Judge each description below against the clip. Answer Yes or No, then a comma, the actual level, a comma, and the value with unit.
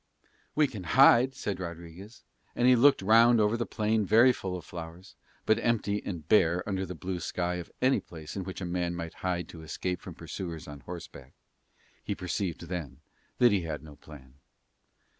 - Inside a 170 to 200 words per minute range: Yes, average, 190 wpm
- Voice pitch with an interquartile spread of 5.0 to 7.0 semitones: No, average, 4.4 semitones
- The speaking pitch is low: Yes, very low, 90 Hz